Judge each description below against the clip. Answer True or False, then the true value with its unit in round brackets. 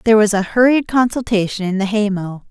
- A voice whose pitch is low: False (210 Hz)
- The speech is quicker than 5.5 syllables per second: True (5.9 syllables/s)